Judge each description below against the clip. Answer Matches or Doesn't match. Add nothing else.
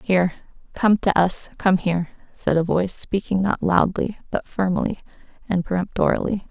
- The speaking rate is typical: Matches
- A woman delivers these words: Matches